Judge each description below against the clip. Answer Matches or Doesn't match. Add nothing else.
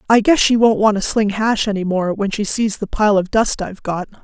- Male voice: Doesn't match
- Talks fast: Matches